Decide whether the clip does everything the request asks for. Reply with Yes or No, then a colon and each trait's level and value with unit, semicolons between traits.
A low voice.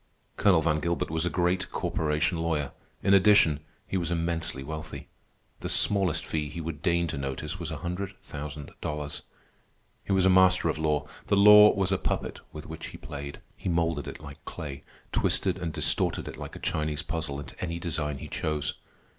Yes: very low, 80 Hz